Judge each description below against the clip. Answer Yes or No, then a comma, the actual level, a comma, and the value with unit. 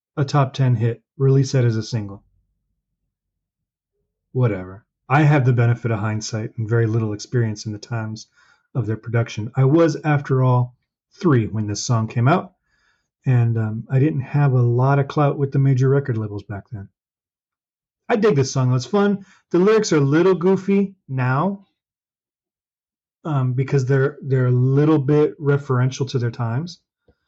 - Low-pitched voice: Yes, low, 130 Hz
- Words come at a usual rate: Yes, average, 165 wpm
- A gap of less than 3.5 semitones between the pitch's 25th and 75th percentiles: No, average, 3.9 semitones